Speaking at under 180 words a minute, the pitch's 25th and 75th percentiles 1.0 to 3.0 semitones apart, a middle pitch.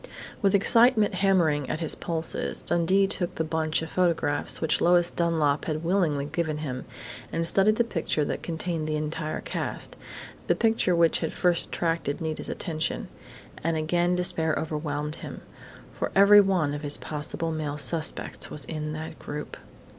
Yes: average, 160 wpm; narrow, 2.5 semitones; medium, 160 Hz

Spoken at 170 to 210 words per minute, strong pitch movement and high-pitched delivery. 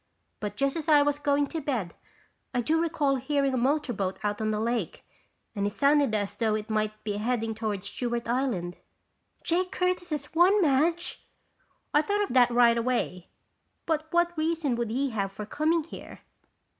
Yes: average, 180 wpm; wide, 6.1 semitones; very high, 260 Hz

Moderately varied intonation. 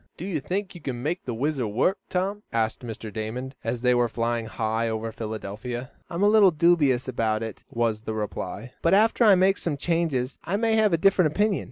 No: wide, 8.1 semitones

